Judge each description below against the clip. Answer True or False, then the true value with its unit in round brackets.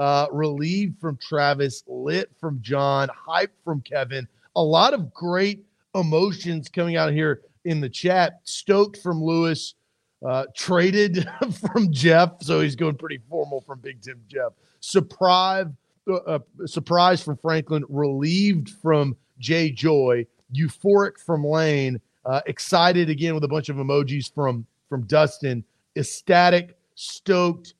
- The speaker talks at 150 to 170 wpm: False (135 wpm)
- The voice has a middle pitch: True (160 Hz)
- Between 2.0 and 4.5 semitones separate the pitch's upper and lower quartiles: True (4.1 semitones)